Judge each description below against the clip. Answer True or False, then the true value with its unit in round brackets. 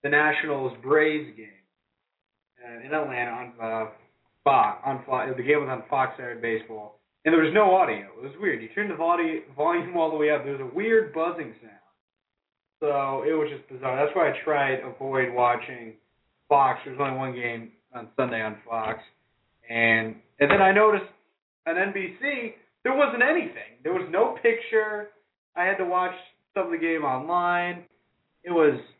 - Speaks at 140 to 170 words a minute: False (180 wpm)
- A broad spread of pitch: True (6.5 semitones)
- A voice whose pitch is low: False (145 Hz)